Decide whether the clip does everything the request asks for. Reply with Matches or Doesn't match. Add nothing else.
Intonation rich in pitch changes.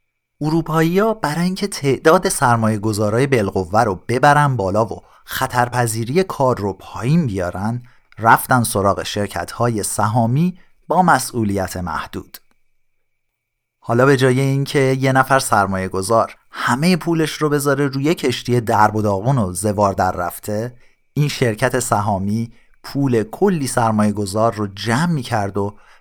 Doesn't match